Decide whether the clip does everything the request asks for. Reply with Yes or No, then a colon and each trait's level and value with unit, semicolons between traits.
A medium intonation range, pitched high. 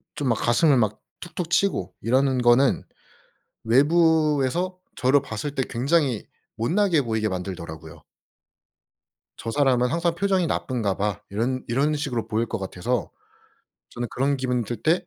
No: average, 5.0 semitones; low, 130 Hz